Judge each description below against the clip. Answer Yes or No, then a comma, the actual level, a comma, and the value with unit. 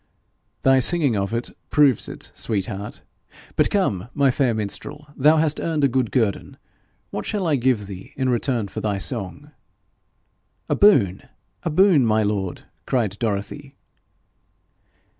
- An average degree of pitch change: No, wide, 5.8 semitones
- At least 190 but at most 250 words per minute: No, average, 145 wpm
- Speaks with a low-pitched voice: Yes, low, 125 Hz